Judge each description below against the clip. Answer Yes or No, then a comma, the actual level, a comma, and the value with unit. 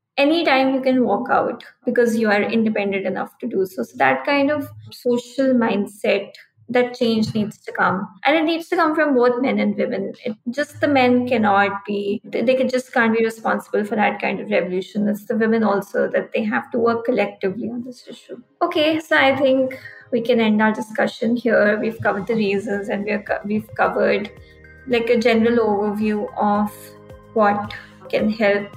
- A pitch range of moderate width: Yes, average, 3.8 semitones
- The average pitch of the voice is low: No, high, 230 Hz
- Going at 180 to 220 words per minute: Yes, average, 190 wpm